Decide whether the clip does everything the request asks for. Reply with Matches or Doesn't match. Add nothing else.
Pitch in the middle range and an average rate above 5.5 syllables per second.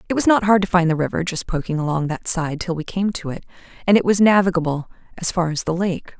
Matches